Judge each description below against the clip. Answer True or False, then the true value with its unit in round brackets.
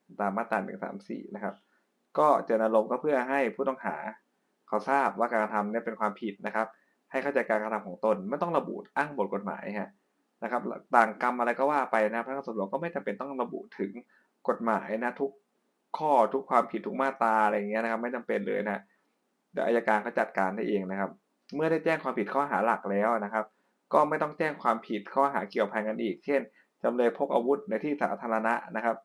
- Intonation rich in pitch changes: False (3.8 semitones)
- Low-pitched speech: True (115 Hz)